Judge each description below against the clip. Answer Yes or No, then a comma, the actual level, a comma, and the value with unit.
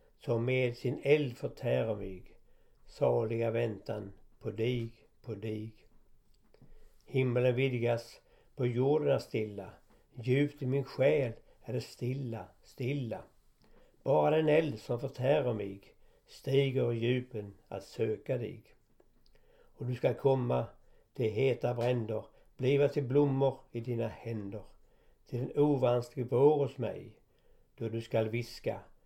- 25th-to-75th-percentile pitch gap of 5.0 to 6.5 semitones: No, average, 3.3 semitones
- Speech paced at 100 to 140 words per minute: Yes, slow, 125 wpm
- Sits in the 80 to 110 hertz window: No, low, 120 Hz